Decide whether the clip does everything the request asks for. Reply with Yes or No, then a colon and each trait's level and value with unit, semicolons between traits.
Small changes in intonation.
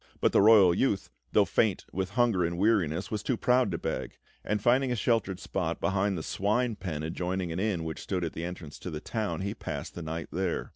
No: average, 4.0 semitones